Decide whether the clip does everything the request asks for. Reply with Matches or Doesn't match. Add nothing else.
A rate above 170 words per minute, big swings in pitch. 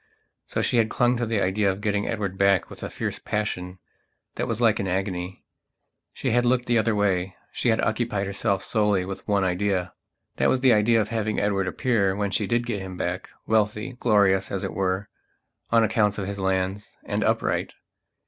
Doesn't match